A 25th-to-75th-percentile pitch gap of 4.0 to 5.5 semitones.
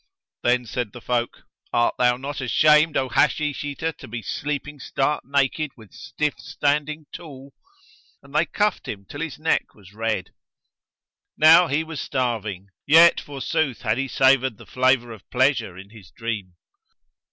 Yes: average, 4.3 semitones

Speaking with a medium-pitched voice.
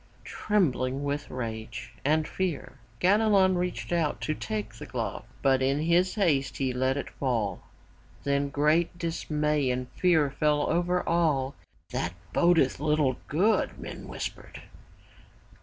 Yes: medium, 150 Hz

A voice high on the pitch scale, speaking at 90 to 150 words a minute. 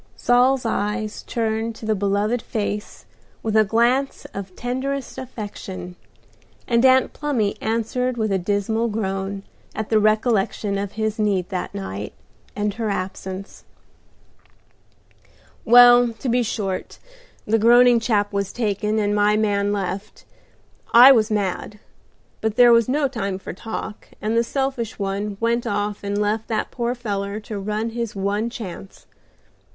Yes: high, 215 Hz; average, 145 wpm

